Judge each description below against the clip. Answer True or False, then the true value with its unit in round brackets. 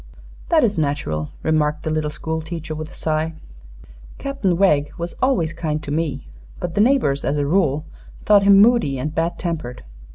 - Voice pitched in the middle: True (160 Hz)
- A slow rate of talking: False (175 wpm)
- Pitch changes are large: False (4.1 semitones)